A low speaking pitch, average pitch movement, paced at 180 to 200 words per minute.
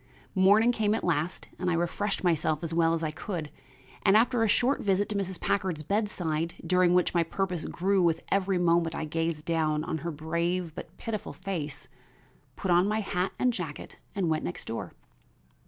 No: medium, 175 Hz; average, 3.3 semitones; average, 190 wpm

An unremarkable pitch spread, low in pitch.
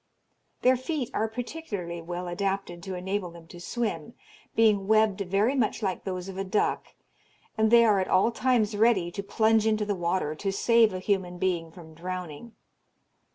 No: average, 3.7 semitones; high, 195 Hz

